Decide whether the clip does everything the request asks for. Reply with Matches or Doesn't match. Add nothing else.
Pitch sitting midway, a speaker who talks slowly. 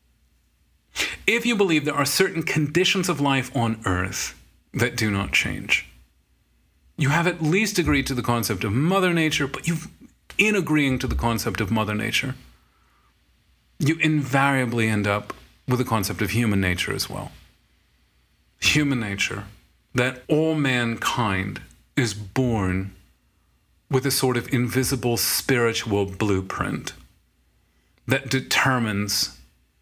Doesn't match